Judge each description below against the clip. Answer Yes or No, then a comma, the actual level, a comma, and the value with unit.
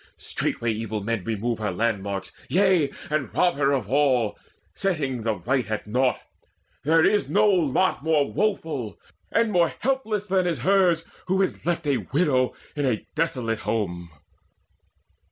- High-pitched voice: No, medium, 140 Hz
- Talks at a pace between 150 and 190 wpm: Yes, average, 155 wpm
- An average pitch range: No, wide, 7.8 semitones